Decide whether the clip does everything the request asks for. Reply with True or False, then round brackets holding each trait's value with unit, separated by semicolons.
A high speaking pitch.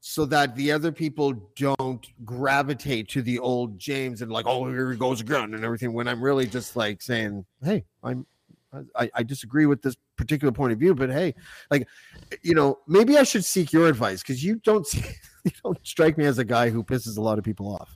False (130 Hz)